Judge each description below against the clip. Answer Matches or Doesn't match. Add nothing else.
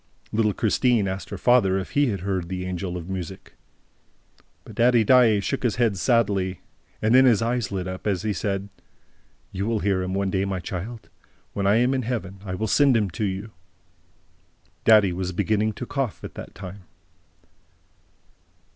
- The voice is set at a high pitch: Doesn't match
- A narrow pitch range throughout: Doesn't match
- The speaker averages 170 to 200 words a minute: Matches